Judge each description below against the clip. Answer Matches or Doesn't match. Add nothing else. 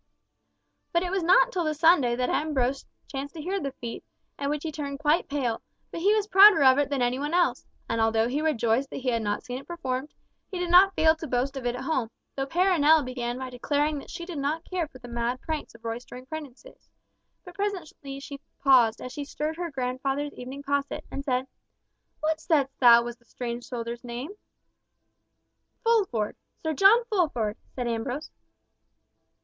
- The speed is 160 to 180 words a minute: Doesn't match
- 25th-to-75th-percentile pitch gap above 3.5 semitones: Matches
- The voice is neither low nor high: Doesn't match